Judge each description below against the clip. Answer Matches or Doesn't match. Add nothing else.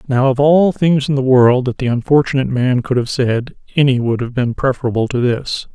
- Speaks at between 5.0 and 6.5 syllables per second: Matches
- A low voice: Matches